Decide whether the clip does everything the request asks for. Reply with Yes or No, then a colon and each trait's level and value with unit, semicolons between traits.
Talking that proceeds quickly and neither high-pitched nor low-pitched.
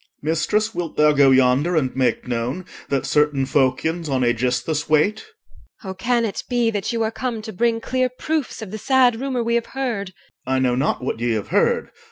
Yes: fast, 215 wpm; medium, 175 Hz